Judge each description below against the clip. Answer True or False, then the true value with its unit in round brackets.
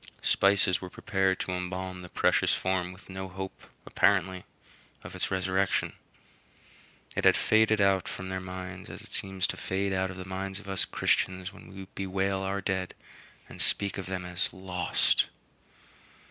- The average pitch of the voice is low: True (95 Hz)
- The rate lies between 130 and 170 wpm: True (165 wpm)